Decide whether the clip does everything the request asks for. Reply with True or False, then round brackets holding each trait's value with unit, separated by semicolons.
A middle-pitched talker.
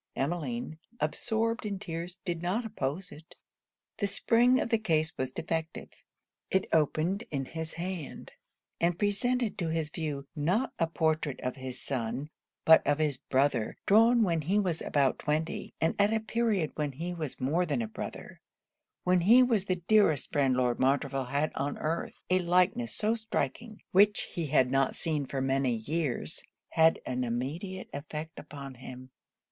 True (160 Hz)